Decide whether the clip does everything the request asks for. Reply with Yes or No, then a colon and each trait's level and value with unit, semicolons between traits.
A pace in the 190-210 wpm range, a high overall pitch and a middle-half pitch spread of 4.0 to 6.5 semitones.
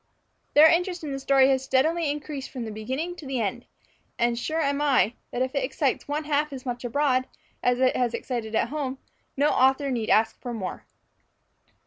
No: average, 195 wpm; very high, 265 Hz; average, 3.1 semitones